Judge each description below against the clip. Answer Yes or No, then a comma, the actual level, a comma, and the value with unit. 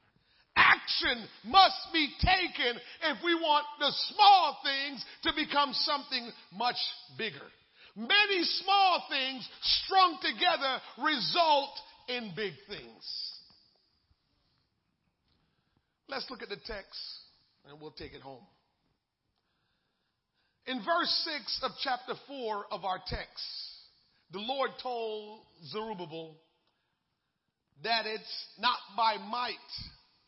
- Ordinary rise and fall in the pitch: No, wide, 6.5 semitones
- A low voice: No, very high, 255 Hz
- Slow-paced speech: Yes, slow, 105 wpm